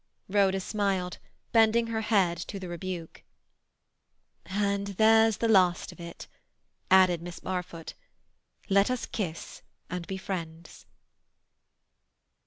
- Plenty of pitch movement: No, average, 2.8 semitones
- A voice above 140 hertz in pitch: Yes, high, 190 Hz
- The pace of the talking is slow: Yes, slow, 110 wpm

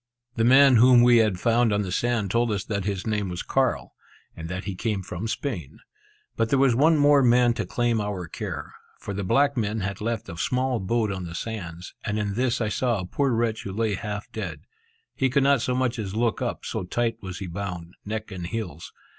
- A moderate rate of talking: No, fast, 225 wpm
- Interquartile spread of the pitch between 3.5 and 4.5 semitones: Yes, average, 4.0 semitones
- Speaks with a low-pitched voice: Yes, low, 110 Hz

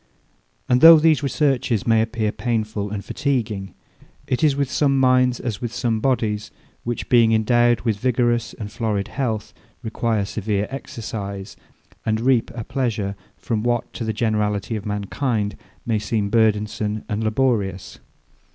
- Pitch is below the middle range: Yes, low, 115 Hz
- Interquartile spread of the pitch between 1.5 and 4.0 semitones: Yes, average, 2.8 semitones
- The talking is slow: No, average, 145 wpm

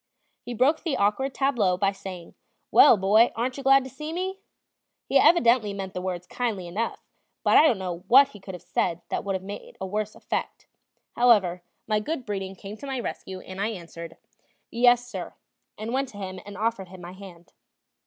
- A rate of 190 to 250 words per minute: Yes, average, 200 wpm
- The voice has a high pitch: Yes, high, 205 Hz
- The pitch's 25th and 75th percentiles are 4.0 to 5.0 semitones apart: Yes, average, 4.6 semitones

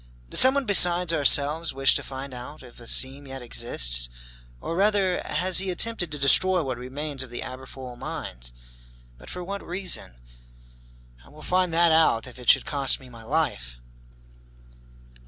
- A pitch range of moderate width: No, wide, 6.0 semitones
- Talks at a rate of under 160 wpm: No, average, 165 wpm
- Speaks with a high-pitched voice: No, medium, 140 Hz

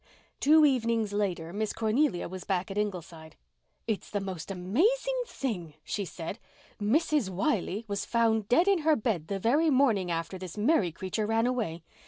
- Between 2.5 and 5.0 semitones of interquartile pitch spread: No, wide, 5.4 semitones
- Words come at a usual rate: Yes, average, 165 wpm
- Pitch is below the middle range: No, high, 210 Hz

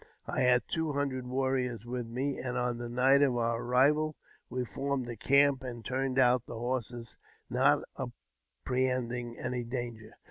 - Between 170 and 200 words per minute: No, average, 155 wpm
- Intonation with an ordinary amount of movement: No, narrow, 1.7 semitones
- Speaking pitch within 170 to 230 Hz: No, low, 125 Hz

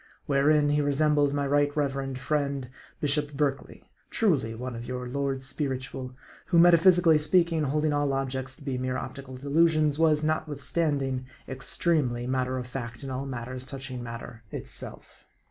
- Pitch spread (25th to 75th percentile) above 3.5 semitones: No, average, 2.7 semitones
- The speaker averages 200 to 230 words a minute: No, average, 150 wpm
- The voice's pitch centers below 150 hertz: Yes, medium, 140 Hz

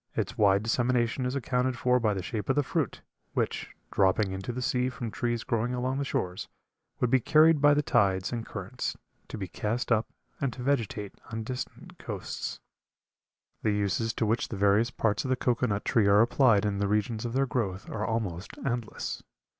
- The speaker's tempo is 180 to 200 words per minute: Yes, average, 195 wpm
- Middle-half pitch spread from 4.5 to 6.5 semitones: No, average, 3.4 semitones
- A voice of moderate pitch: No, low, 115 Hz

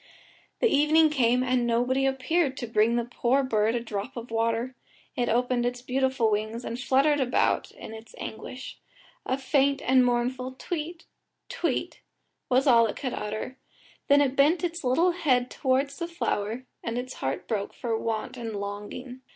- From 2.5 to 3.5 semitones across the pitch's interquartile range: Yes, average, 2.8 semitones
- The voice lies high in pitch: Yes, very high, 250 Hz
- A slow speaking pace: No, average, 165 wpm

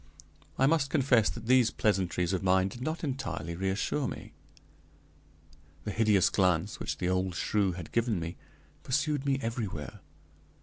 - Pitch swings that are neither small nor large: No, wide, 5.7 semitones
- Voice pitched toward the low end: Yes, low, 105 Hz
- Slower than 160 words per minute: Yes, average, 145 wpm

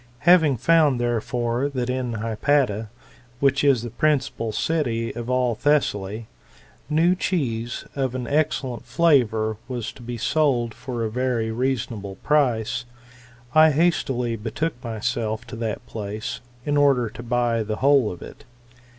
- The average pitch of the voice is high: No, low, 120 Hz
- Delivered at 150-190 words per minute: No, average, 140 wpm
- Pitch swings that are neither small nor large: Yes, average, 3.7 semitones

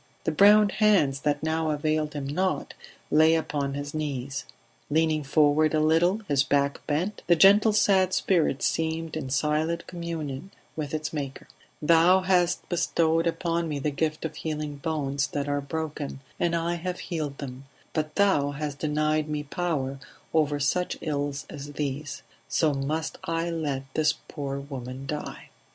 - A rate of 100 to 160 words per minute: Yes, average, 155 wpm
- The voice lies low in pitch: No, medium, 155 Hz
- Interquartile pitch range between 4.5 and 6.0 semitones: No, narrow, 2.6 semitones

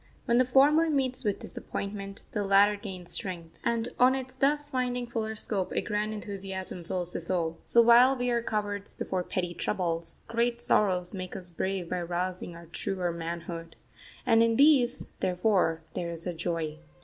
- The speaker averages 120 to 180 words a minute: Yes, average, 175 wpm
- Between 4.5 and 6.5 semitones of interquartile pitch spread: Yes, average, 5.0 semitones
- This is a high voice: Yes, high, 200 Hz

